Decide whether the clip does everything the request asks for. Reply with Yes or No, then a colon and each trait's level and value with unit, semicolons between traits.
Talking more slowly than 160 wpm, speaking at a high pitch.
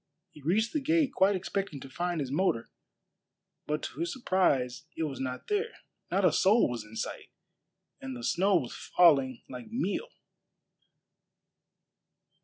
No: average, 150 wpm; medium, 175 Hz